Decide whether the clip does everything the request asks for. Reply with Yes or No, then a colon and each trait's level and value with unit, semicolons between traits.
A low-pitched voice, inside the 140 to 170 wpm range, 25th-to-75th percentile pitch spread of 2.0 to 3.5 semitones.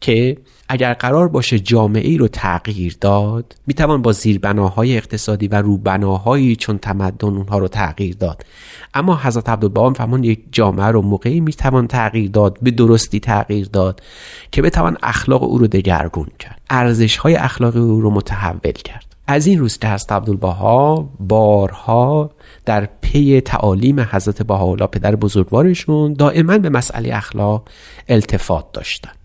No: low, 110 Hz; average, 145 wpm; average, 4.1 semitones